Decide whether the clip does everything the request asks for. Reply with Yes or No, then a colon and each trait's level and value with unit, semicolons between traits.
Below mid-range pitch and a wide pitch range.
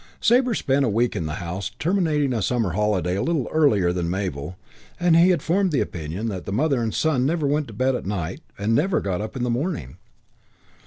Yes: low, 120 Hz; wide, 8.6 semitones